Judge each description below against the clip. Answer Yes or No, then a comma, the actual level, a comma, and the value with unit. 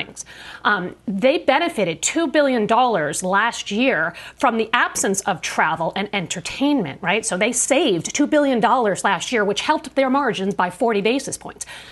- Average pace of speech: Yes, average, 150 wpm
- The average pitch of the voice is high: Yes, high, 230 Hz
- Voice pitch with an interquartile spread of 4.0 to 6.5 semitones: Yes, average, 5.0 semitones